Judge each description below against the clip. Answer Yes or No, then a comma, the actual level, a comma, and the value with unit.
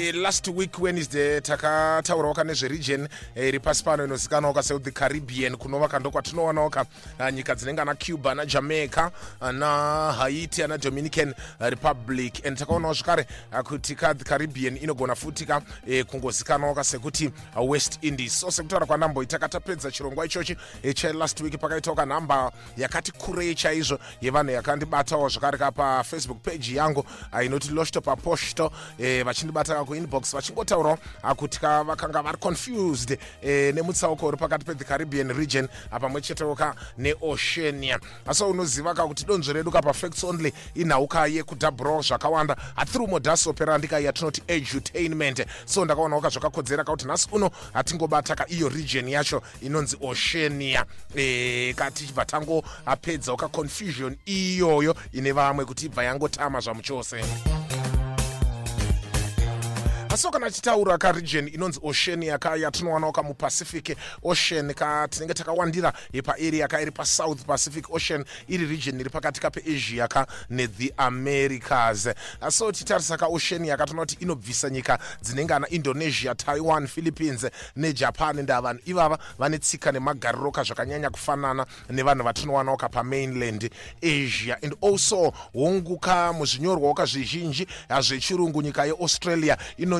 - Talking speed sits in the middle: No, slow, 125 wpm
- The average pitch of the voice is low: No, medium, 150 Hz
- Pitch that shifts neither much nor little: Yes, average, 3.1 semitones